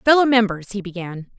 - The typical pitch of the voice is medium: No, high, 210 Hz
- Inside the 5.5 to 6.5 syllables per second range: Yes, 5.6 syllables/s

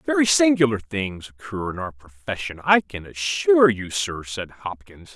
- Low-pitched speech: Yes, low, 115 Hz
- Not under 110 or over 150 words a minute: No, average, 165 wpm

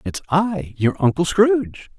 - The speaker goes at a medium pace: Yes, average, 150 wpm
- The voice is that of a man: Yes, male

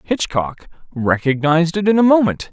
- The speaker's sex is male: Yes, male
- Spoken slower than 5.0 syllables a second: No, 5.1 syllables/s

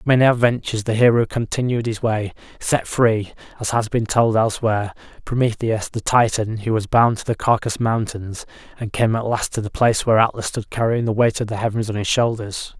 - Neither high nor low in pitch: No, low, 110 Hz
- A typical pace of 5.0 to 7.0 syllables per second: Yes, 5.7 syllables/s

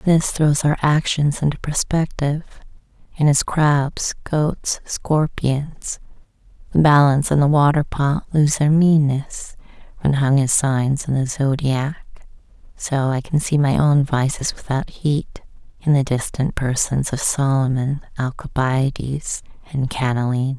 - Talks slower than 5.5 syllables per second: Yes, 4.0 syllables/s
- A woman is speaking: Yes, female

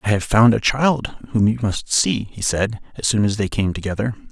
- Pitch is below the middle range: Yes, low, 110 Hz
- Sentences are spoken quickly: Yes, fast, 235 wpm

